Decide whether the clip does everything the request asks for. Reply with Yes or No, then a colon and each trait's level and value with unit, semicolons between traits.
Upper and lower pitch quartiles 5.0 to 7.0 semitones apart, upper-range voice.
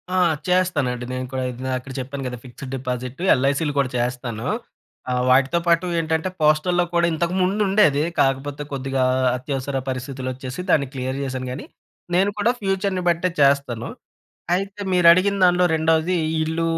No: average, 5.3 semitones; medium, 140 Hz